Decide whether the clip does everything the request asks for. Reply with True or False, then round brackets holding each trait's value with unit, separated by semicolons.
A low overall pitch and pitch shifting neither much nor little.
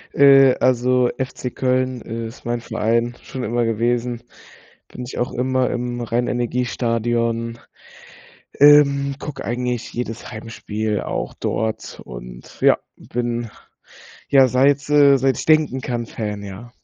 False (120 Hz; 2.0 semitones)